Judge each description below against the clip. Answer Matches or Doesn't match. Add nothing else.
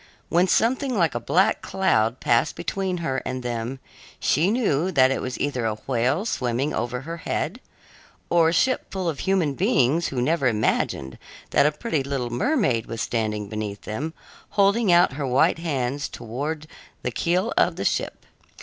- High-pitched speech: Doesn't match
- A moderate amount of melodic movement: Doesn't match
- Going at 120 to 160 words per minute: Doesn't match